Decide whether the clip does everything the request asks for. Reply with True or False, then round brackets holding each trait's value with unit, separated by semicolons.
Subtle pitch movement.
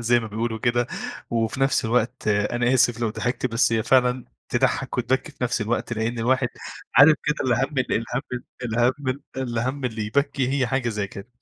True (2.2 semitones)